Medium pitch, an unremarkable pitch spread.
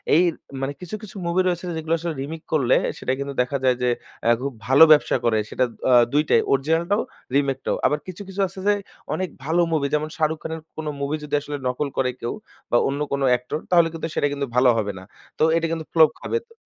Yes: medium, 150 Hz; average, 3.4 semitones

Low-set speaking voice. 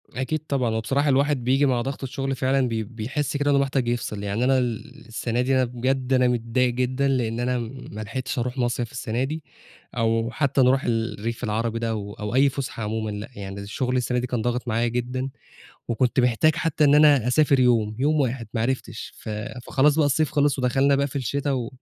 Yes: low, 125 Hz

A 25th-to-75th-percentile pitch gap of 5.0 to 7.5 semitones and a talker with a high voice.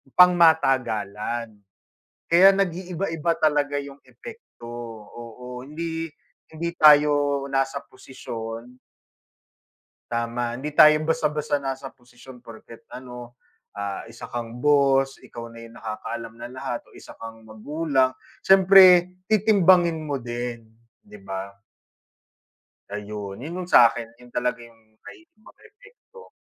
No: wide, 5.6 semitones; low, 135 Hz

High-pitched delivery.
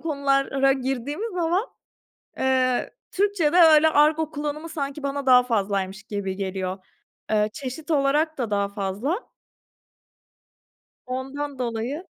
Yes: very high, 275 Hz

